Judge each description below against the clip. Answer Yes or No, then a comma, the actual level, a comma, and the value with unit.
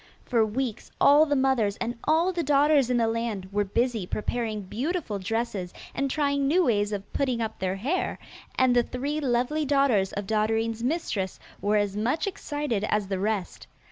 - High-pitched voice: Yes, high, 235 Hz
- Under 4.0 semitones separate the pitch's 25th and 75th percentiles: No, average, 5.2 semitones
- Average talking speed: Yes, average, 175 wpm